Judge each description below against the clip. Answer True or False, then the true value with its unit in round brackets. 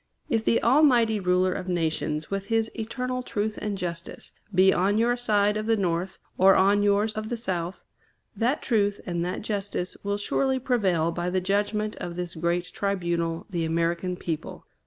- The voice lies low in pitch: False (195 Hz)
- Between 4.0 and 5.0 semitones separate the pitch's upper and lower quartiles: False (3.6 semitones)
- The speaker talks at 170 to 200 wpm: True (175 wpm)